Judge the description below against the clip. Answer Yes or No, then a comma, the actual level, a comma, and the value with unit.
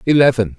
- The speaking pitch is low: Yes, low, 120 Hz